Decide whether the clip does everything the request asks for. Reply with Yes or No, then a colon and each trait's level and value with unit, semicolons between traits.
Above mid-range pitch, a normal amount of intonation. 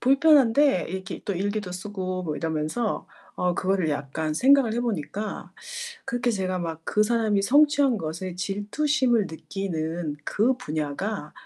No: high, 195 Hz; wide, 6.3 semitones